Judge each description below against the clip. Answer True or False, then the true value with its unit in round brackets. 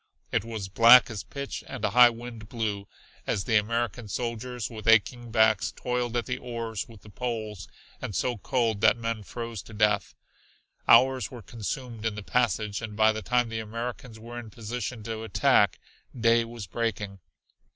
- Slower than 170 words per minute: False (175 wpm)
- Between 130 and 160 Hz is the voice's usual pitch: False (115 Hz)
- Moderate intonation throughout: False (2.0 semitones)